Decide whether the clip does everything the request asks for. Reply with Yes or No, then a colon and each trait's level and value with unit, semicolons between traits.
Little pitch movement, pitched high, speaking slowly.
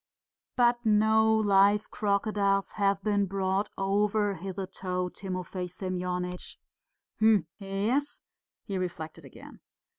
Yes: narrow, 2.2 semitones; high, 195 Hz; slow, 95 wpm